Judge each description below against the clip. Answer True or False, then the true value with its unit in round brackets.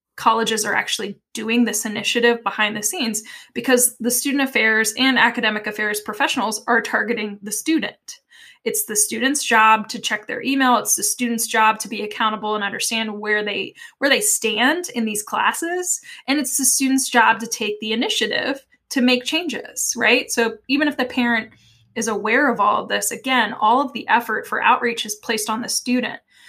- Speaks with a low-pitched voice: False (230 Hz)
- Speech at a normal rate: True (185 wpm)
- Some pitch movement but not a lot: True (3.3 semitones)